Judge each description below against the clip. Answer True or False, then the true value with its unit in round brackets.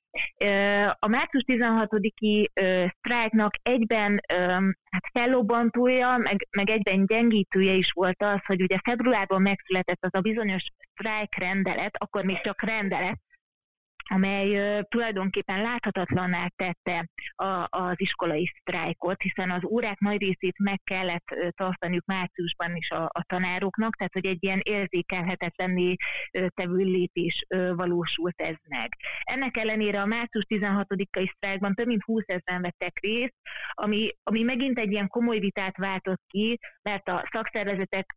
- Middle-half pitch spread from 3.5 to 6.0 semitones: False (2.8 semitones)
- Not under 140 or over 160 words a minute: False (125 wpm)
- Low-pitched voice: False (195 Hz)